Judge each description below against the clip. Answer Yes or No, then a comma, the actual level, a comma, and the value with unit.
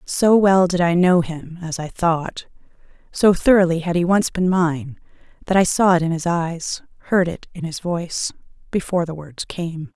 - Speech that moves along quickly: No, average, 195 wpm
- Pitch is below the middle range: No, medium, 175 Hz